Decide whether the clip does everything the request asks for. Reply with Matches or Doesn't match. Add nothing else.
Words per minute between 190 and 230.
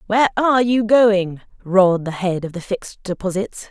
Doesn't match